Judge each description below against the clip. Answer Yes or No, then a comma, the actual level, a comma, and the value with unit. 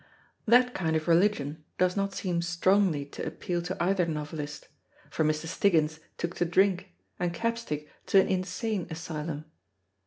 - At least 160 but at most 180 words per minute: No, average, 150 wpm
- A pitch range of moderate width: Yes, average, 3.5 semitones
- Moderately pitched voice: Yes, medium, 175 Hz